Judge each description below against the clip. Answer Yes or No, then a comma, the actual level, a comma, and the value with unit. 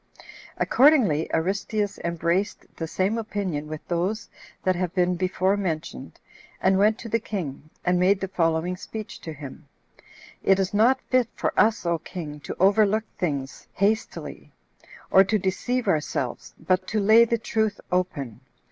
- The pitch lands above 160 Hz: Yes, medium, 185 Hz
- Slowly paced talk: No, average, 150 wpm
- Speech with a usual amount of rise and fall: Yes, average, 4.1 semitones